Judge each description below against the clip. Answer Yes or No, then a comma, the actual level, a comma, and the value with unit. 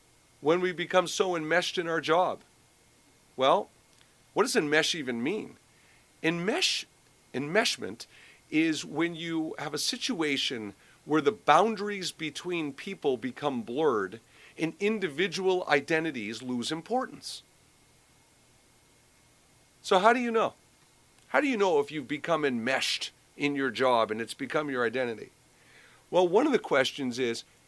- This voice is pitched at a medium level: Yes, medium, 160 Hz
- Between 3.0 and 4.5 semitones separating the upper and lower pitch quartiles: No, average, 5.0 semitones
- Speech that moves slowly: Yes, slow, 130 wpm